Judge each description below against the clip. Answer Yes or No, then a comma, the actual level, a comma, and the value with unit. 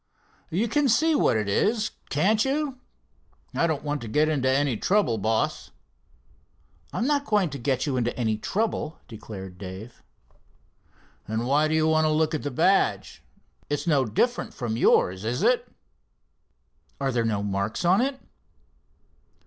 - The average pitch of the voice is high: No, medium, 145 Hz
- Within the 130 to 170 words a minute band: Yes, average, 155 wpm